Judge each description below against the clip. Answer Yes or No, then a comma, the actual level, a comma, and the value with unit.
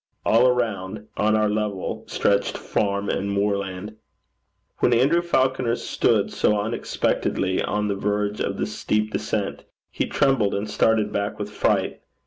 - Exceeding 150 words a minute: No, average, 140 wpm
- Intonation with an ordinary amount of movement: No, narrow, 2.0 semitones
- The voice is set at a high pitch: No, low, 105 Hz